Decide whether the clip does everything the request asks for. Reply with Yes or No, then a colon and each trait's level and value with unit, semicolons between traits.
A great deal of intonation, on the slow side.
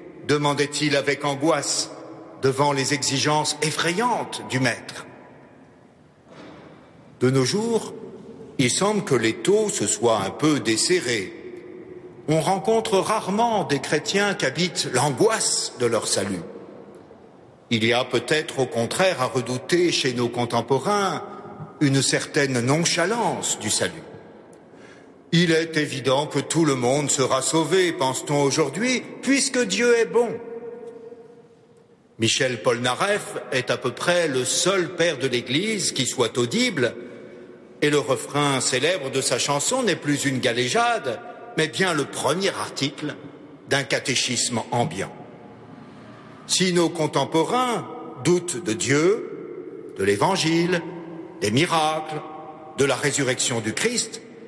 Yes: wide, 7.1 semitones; slow, 125 wpm